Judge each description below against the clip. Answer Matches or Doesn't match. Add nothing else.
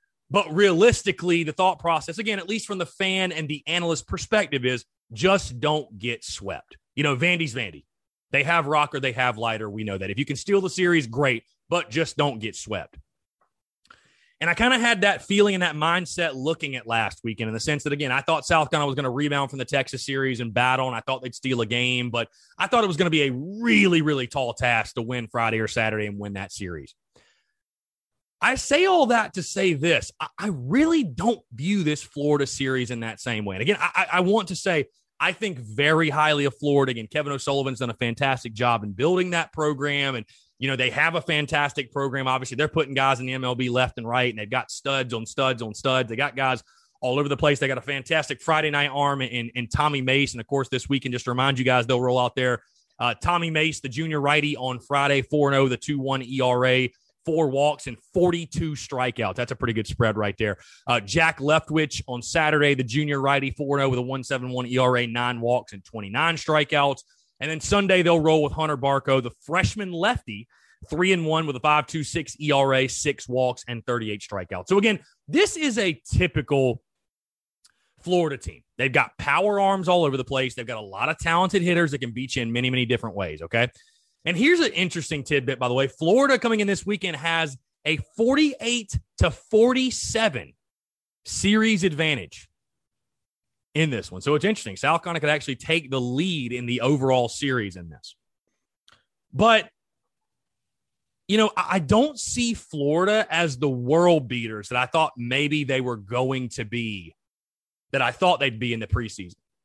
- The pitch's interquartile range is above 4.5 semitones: Matches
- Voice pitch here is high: Doesn't match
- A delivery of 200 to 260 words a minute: Matches